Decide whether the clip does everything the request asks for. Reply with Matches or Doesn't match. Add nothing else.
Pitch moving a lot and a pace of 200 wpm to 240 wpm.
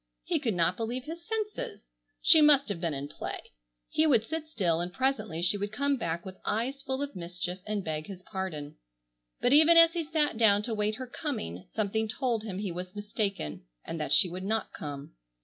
Matches